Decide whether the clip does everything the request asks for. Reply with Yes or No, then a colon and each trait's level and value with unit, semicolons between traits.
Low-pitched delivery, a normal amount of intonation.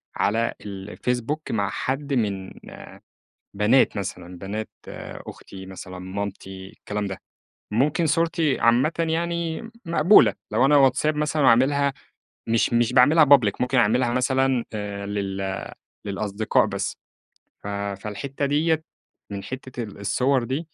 No: low, 120 Hz; wide, 5.8 semitones